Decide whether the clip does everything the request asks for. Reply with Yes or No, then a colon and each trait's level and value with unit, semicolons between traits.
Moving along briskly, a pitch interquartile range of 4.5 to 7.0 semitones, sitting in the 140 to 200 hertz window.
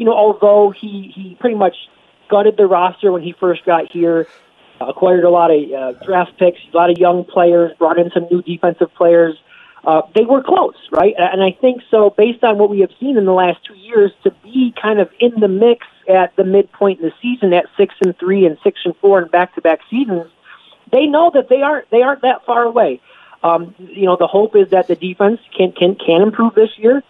No: fast, 225 wpm; average, 3.7 semitones; high, 190 Hz